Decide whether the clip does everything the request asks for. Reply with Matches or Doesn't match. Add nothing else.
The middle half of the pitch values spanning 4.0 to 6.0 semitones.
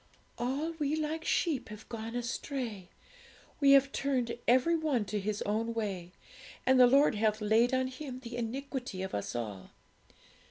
Matches